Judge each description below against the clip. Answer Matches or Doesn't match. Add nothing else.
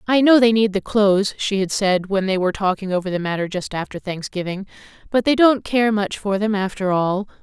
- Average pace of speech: Doesn't match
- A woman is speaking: Matches